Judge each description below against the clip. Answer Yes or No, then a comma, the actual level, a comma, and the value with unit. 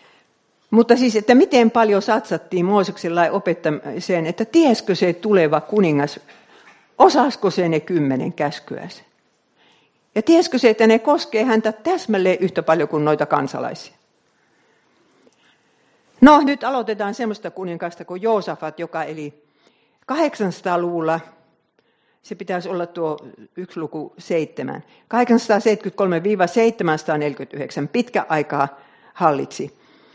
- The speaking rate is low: No, average, 105 wpm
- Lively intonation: Yes, wide, 5.8 semitones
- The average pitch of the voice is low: No, medium, 185 Hz